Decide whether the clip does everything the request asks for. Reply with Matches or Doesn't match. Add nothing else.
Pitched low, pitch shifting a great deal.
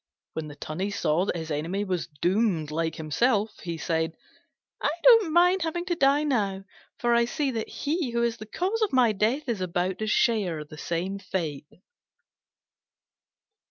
Doesn't match